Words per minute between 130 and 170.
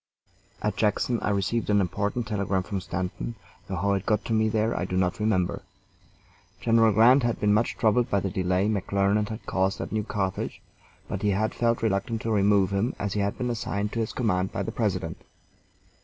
No: average, 200 wpm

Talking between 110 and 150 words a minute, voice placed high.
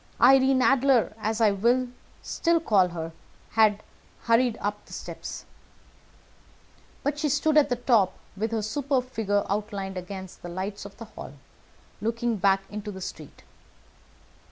Yes: average, 145 wpm; high, 215 Hz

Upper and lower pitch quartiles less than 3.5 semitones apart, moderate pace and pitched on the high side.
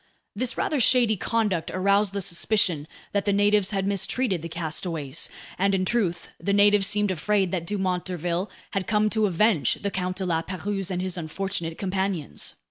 Yes: narrow, 2.6 semitones; average, 175 wpm; high, 195 Hz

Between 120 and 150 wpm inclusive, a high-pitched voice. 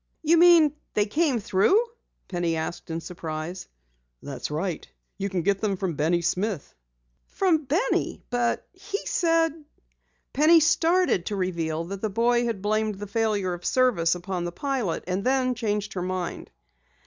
No: average, 160 wpm; high, 205 Hz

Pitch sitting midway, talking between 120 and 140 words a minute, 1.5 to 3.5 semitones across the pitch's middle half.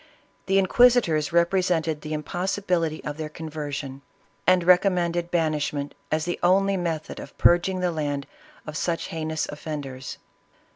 Yes: medium, 165 Hz; slow, 135 wpm; average, 2.9 semitones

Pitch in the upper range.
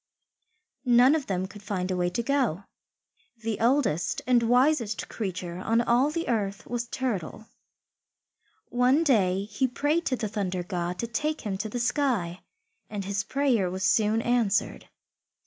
Yes: high, 225 Hz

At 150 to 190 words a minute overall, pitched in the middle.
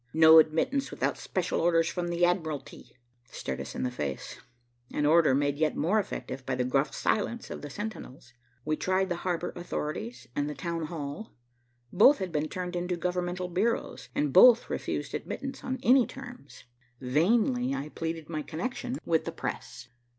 Yes: average, 170 wpm; medium, 165 Hz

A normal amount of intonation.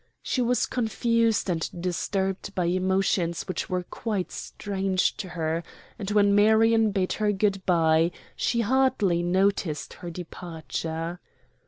Yes: average, 3.4 semitones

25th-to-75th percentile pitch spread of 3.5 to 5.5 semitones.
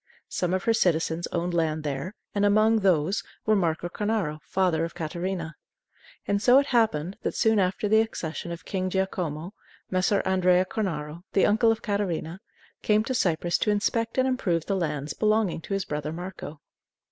Yes: average, 4.2 semitones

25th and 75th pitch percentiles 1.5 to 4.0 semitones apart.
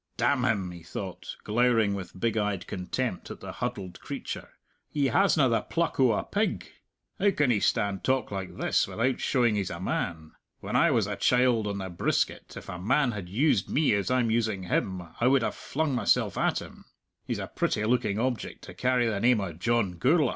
No: average, 4.6 semitones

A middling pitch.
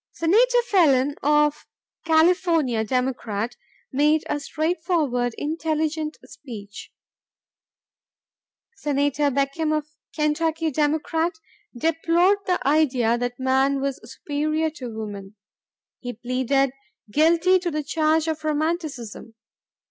No: very high, 300 Hz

